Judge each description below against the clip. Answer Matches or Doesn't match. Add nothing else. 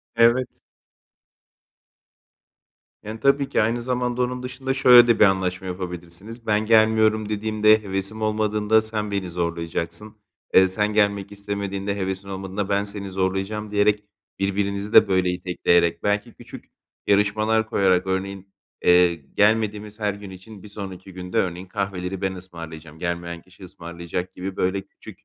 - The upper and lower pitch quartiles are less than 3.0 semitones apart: Matches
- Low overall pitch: Matches